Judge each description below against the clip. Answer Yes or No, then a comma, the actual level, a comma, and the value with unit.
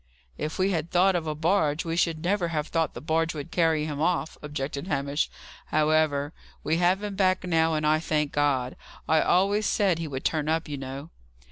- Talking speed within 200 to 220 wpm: Yes, fast, 205 wpm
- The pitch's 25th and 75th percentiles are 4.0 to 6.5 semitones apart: No, average, 2.7 semitones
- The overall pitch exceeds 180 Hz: No, medium, 160 Hz